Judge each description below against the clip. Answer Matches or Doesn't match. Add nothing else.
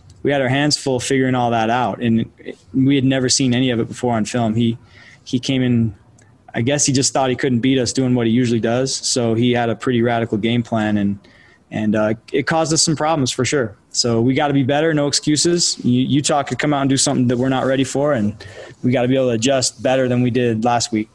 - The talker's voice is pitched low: Matches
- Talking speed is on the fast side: Matches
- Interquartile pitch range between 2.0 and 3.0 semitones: Matches